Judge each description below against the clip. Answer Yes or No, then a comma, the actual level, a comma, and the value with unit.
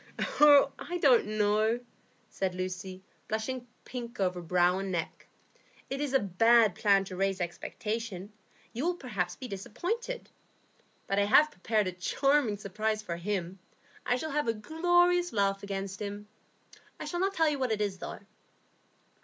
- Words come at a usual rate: Yes, average, 160 wpm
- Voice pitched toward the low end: No, high, 215 Hz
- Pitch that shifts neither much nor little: No, wide, 5.9 semitones